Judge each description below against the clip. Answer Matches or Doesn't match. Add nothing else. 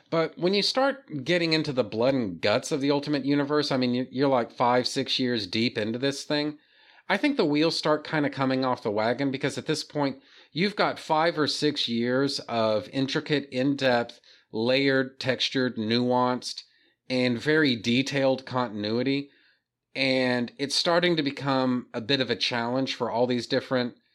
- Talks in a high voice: Doesn't match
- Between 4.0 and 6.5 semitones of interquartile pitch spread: Doesn't match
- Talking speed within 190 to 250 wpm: Doesn't match